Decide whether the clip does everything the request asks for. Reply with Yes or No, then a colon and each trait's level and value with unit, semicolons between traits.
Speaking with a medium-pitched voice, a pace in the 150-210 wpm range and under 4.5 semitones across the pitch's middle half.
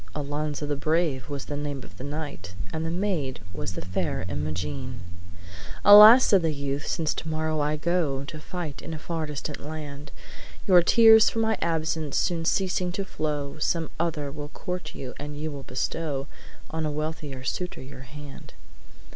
Yes: medium, 150 Hz; average, 170 wpm; average, 2.8 semitones